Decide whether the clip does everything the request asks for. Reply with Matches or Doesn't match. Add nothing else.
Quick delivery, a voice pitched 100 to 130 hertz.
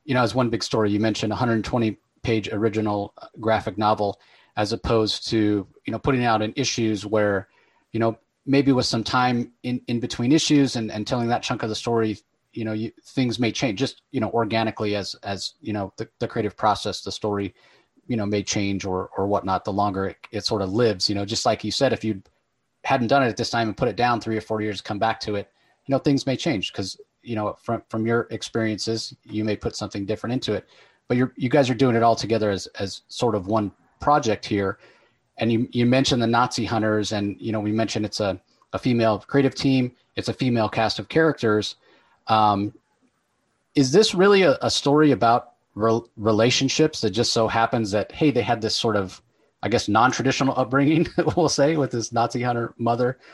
Matches